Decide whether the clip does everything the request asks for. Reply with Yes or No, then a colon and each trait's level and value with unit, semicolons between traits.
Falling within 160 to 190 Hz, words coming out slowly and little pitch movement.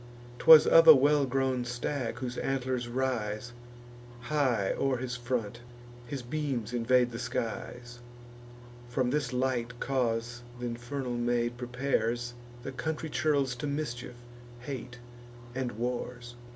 No: low, 125 Hz; slow, 125 wpm; narrow, 1.8 semitones